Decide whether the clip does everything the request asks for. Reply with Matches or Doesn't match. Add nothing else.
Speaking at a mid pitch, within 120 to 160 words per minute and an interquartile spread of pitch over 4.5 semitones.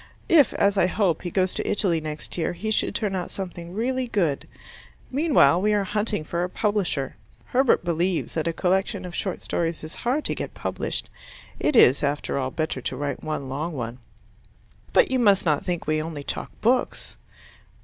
Doesn't match